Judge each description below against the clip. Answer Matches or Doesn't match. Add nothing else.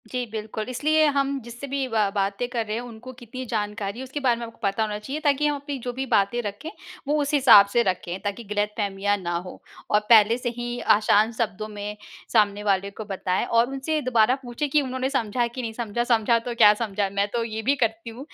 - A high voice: Matches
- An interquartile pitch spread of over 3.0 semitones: Matches